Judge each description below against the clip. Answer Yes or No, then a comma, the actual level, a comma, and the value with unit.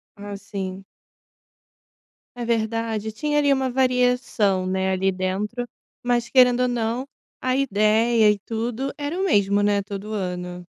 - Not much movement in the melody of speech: No, average, 3.8 semitones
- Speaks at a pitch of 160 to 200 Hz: No, high, 220 Hz